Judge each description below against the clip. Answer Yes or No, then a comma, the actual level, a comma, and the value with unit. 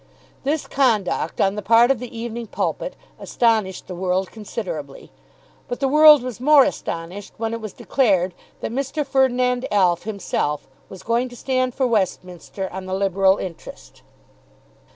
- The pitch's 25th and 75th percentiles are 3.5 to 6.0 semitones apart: Yes, average, 5.1 semitones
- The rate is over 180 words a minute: No, average, 150 wpm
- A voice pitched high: Yes, high, 225 Hz